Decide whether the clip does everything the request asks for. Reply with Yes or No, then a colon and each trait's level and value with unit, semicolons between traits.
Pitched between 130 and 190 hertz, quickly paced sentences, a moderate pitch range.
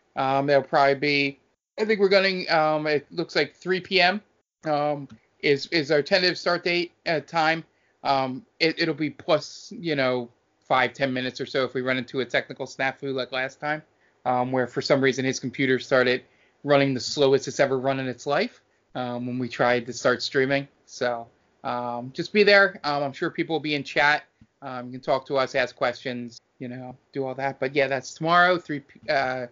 Yes: medium, 140 Hz; fast, 210 wpm; average, 3.3 semitones